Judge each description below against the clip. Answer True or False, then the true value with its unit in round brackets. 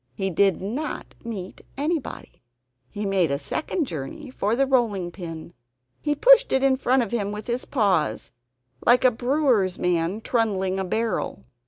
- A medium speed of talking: True (160 wpm)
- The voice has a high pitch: True (215 Hz)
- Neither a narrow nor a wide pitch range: False (5.9 semitones)